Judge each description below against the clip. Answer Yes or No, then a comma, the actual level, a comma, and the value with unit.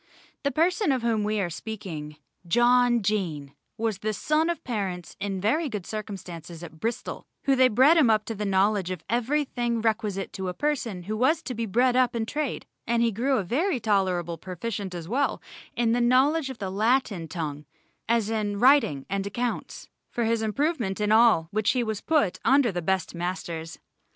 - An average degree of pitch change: Yes, average, 4.6 semitones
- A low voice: No, high, 220 Hz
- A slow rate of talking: No, average, 190 wpm